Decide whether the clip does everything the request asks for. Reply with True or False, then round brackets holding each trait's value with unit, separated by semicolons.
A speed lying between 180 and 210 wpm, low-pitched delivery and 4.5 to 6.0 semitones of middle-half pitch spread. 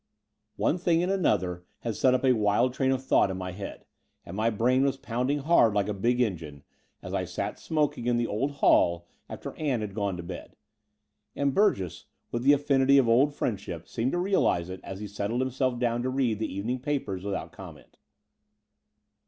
True (195 wpm; 120 Hz; 5.1 semitones)